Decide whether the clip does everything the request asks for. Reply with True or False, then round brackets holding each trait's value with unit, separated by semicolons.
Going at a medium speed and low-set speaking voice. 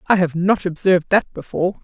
False (195 wpm; 185 Hz)